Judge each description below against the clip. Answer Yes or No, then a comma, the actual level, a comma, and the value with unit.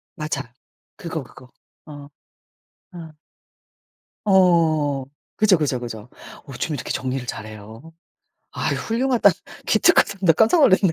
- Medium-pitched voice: Yes, medium, 155 Hz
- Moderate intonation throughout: No, wide, 6.1 semitones